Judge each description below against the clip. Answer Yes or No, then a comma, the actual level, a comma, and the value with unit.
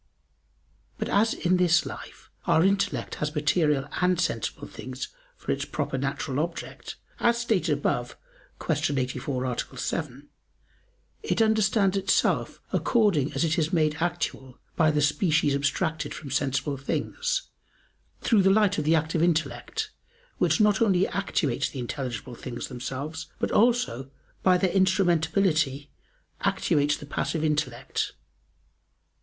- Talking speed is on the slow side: Yes, slow, 130 wpm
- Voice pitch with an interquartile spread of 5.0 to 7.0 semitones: Yes, wide, 5.4 semitones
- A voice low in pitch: No, medium, 160 Hz